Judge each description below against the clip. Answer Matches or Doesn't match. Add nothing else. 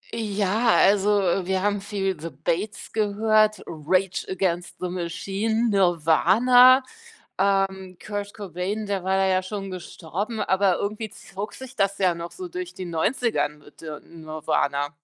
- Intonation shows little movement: Doesn't match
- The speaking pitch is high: Matches